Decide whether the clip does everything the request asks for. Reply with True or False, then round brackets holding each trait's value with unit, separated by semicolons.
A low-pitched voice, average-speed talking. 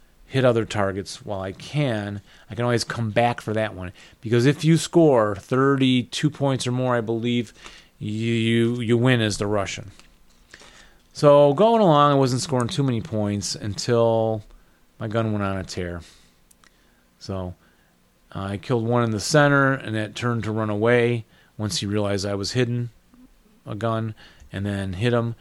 True (115 Hz; 170 wpm)